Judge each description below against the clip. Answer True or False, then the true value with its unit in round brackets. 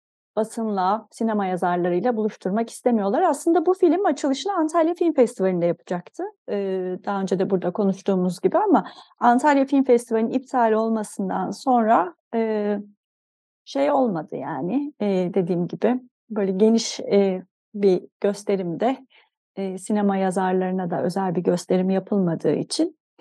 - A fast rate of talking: False (125 wpm)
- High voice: True (210 Hz)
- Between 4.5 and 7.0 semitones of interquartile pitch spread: True (5.2 semitones)